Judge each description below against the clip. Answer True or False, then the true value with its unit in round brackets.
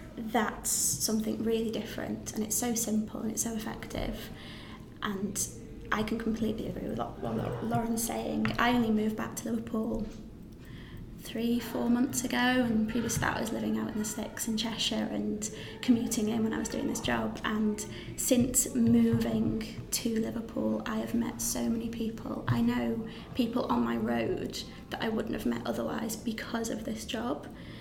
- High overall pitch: True (225 Hz)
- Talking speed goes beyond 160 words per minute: True (175 wpm)